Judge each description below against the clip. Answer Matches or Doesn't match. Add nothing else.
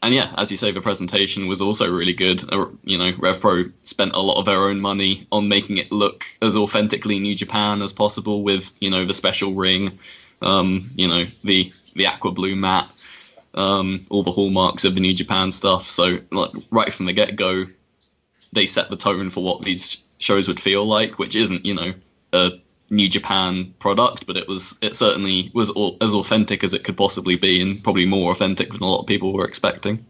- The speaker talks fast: Matches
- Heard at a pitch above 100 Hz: Doesn't match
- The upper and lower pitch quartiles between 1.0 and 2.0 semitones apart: Matches